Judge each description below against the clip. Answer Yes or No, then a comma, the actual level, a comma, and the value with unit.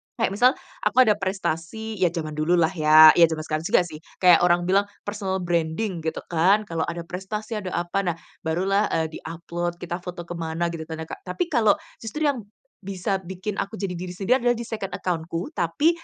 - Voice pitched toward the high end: No, medium, 180 Hz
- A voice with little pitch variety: No, average, 3.6 semitones